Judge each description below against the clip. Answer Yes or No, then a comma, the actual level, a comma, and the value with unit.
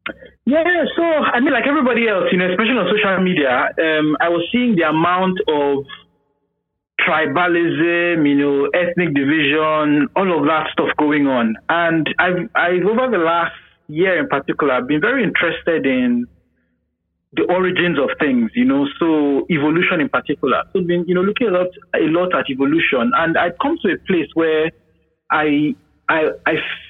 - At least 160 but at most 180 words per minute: Yes, average, 170 wpm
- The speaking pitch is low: No, medium, 170 Hz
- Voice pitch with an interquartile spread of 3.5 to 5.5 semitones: Yes, average, 4.1 semitones